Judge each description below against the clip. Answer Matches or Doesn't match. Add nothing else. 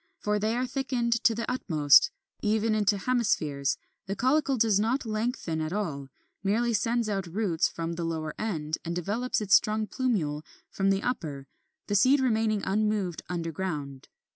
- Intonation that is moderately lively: Doesn't match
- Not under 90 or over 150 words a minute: Doesn't match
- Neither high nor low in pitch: Doesn't match